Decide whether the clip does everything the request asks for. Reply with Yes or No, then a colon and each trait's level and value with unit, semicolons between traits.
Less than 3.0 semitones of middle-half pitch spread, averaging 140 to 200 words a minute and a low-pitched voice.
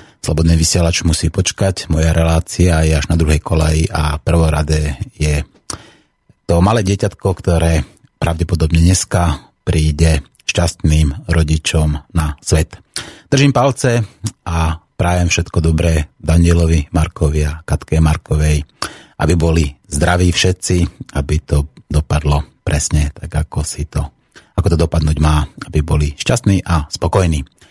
No: narrow, 2.4 semitones; average, 125 wpm; very low, 80 Hz